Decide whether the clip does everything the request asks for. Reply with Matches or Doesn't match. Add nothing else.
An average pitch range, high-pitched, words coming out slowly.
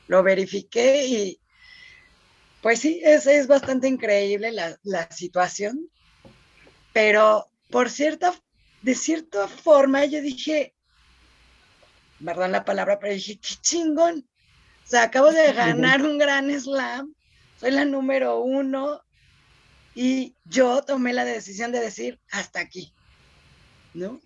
Doesn't match